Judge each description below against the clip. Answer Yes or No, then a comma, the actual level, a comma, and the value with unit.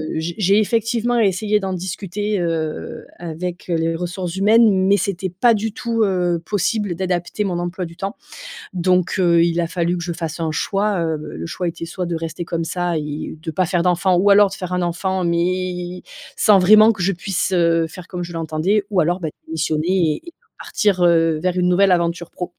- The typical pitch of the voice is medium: Yes, medium, 180 Hz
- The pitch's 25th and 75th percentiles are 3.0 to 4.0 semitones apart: No, narrow, 2.5 semitones